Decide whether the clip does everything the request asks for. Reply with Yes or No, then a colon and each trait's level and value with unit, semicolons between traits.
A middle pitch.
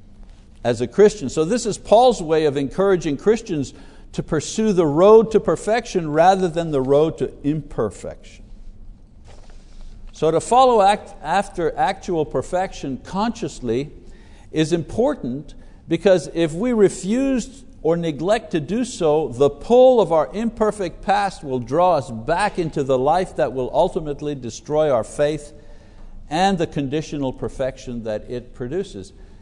Yes: medium, 160 Hz